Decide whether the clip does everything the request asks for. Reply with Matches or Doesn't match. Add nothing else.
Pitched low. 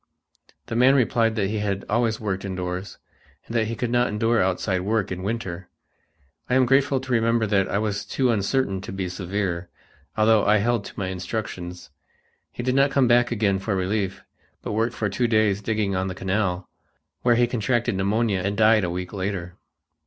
Matches